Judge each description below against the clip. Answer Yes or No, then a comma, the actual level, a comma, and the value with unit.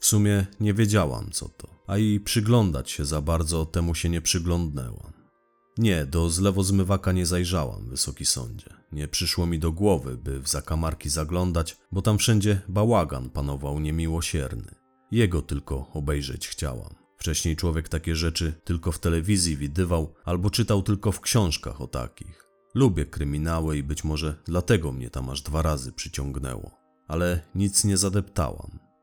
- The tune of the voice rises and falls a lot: No, average, 4.6 semitones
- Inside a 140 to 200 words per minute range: Yes, average, 155 wpm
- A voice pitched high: No, very low, 85 Hz